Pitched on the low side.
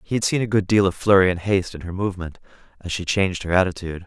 Yes: very low, 95 Hz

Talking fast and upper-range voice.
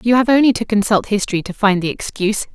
Yes: fast, 235 wpm; high, 210 Hz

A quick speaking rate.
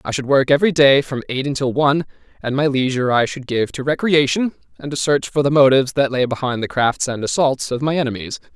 Yes: fast, 230 wpm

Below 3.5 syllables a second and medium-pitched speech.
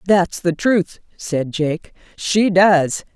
Yes: 2.8 syllables/s; medium, 180 Hz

